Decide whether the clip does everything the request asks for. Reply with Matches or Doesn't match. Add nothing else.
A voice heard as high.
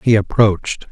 Doesn't match